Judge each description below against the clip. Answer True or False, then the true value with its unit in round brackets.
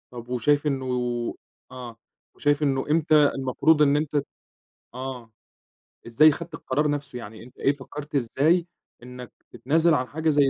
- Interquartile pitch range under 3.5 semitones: True (3.1 semitones)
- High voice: False (140 Hz)